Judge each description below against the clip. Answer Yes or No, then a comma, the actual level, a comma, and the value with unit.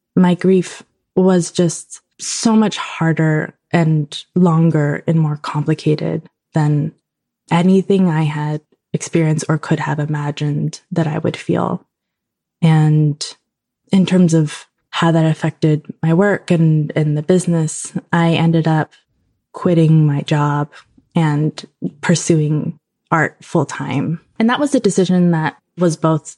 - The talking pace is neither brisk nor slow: No, slow, 125 wpm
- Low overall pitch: No, medium, 160 Hz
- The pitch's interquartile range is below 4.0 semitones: Yes, narrow, 2.5 semitones